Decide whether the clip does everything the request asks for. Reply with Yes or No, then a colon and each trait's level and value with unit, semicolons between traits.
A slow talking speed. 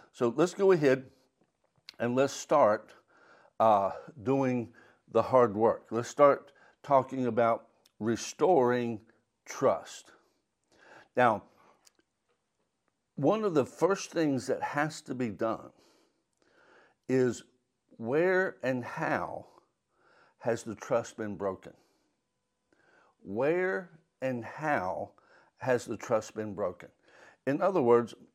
Yes: slow, 105 wpm